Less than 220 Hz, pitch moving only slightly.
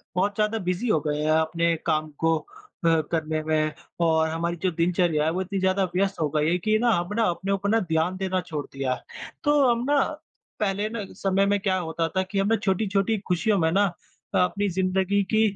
No: medium, 185 Hz; average, 3.7 semitones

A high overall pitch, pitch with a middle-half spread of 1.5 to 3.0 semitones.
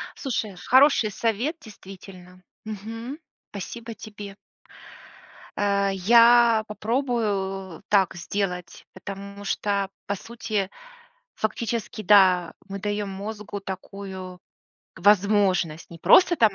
Yes: high, 205 Hz; narrow, 2.5 semitones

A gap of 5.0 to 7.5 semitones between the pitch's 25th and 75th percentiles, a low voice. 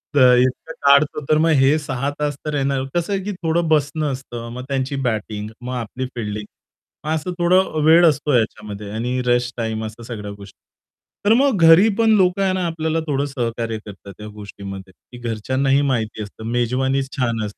Yes: average, 5.3 semitones; low, 130 Hz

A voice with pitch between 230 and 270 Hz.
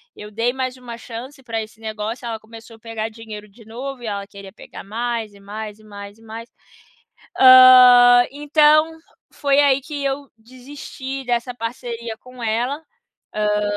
Yes: high, 235 Hz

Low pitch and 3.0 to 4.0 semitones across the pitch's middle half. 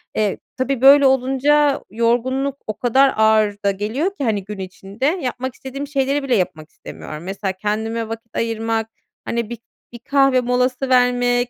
No: high, 245 Hz; average, 3.7 semitones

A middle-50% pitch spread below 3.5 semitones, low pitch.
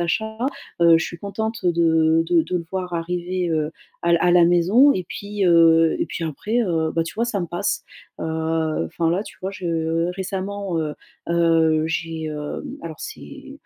No: narrow, 2.4 semitones; medium, 170 Hz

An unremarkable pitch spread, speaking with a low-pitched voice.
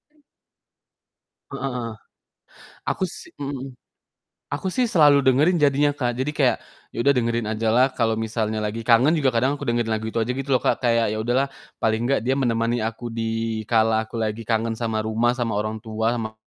Yes: average, 3.3 semitones; low, 120 Hz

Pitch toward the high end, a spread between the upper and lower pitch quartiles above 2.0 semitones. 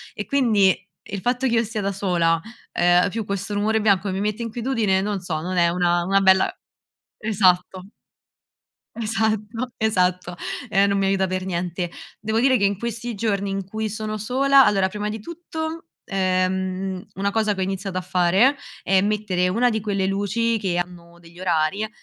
Yes: high, 200 Hz; average, 2.9 semitones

